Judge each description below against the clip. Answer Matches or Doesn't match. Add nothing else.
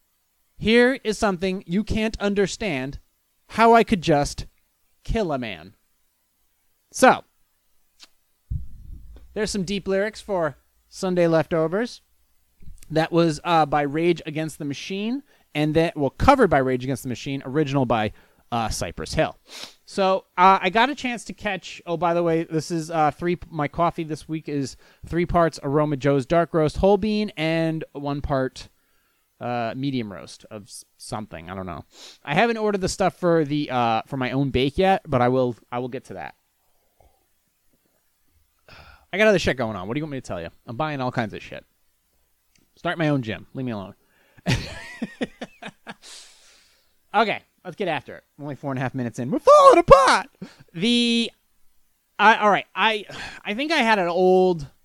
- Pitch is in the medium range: Matches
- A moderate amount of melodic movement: Doesn't match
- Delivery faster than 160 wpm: Matches